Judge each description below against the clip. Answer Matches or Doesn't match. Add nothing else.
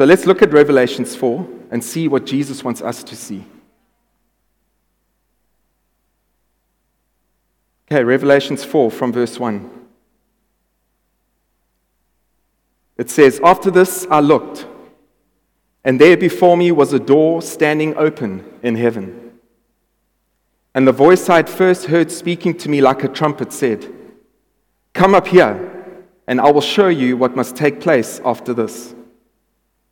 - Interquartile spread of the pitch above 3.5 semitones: Matches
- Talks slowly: Matches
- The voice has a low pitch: Doesn't match